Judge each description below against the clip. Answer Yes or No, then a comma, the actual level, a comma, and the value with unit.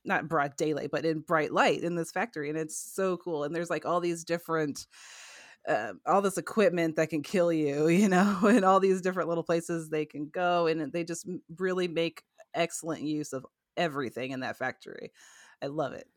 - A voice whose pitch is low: No, medium, 170 Hz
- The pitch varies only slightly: Yes, narrow, 2.2 semitones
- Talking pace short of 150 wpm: No, average, 200 wpm